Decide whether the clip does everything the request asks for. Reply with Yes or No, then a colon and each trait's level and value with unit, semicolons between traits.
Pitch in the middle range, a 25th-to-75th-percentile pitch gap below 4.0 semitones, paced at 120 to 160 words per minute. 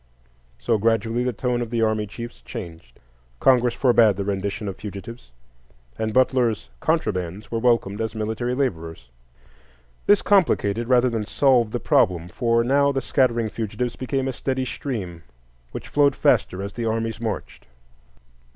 No: low, 115 Hz; average, 3.5 semitones; average, 150 wpm